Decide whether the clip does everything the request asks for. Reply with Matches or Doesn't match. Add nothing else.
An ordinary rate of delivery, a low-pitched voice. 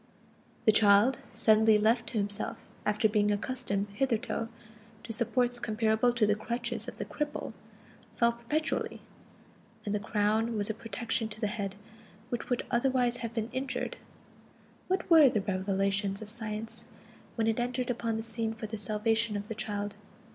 Doesn't match